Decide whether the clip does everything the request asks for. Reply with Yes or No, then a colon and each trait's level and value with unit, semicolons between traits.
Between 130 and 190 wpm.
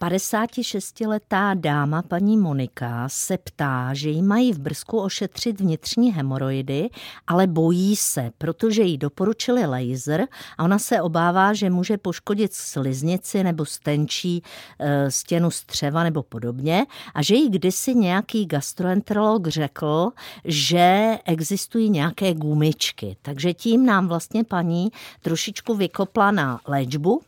No: average, 120 wpm